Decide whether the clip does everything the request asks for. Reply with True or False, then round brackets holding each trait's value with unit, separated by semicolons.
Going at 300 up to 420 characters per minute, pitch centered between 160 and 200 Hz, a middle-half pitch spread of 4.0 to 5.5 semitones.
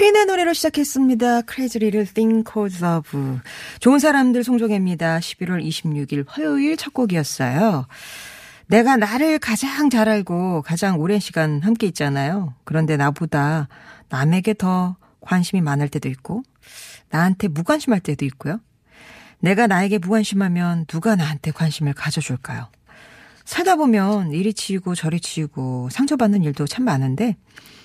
False (340 characters per minute; 185 Hz; 6.2 semitones)